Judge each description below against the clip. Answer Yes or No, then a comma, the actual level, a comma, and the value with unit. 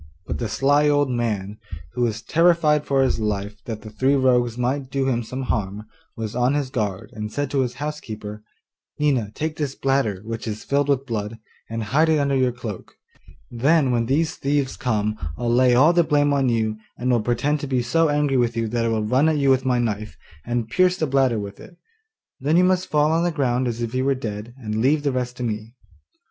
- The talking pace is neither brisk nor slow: No, fast, 225 wpm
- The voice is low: Yes, low, 125 Hz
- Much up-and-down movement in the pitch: No, average, 4.2 semitones